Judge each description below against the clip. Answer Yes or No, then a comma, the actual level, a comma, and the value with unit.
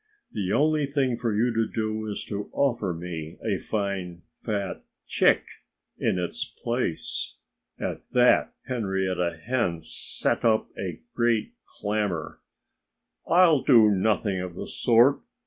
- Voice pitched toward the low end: Yes, low, 110 Hz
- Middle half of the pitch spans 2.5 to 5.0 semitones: Yes, average, 4.7 semitones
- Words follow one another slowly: Yes, slow, 130 wpm